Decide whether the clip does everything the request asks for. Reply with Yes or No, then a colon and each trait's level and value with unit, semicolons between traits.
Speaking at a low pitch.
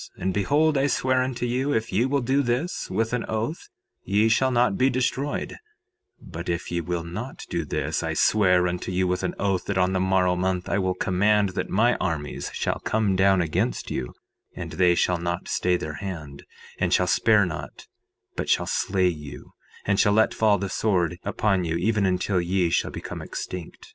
Yes: very low, 95 Hz